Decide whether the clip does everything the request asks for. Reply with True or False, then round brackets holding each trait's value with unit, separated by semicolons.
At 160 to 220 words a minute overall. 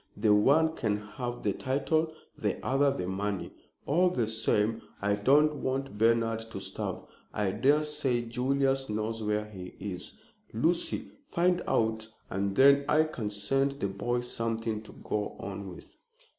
False (150 wpm)